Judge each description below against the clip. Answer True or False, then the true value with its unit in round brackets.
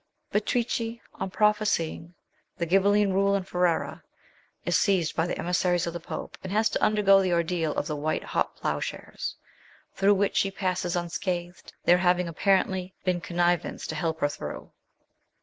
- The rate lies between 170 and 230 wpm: False (160 wpm)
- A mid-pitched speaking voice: True (180 Hz)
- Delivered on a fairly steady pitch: True (2.3 semitones)